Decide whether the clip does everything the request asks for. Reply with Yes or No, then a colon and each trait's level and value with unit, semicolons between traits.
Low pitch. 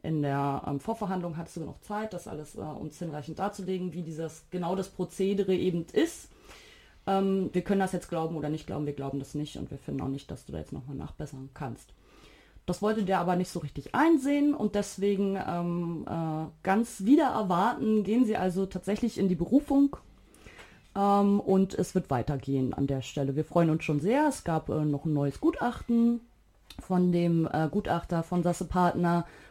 No: medium, 180 Hz